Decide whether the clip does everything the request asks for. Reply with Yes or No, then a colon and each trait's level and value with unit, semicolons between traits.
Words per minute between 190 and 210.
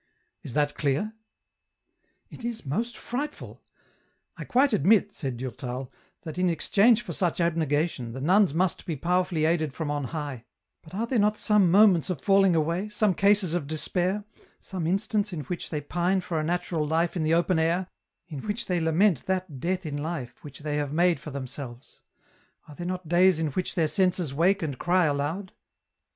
Yes: average, 195 wpm